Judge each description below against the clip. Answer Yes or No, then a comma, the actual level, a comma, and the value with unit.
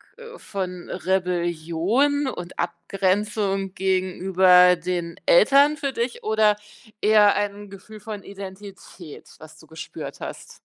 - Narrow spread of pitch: No, average, 3.0 semitones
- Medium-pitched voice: No, high, 195 Hz